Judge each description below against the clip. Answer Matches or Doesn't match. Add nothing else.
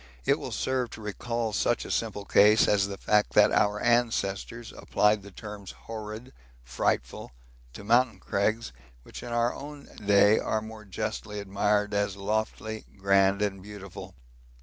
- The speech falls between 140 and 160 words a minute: Matches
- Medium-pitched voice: Doesn't match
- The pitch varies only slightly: Matches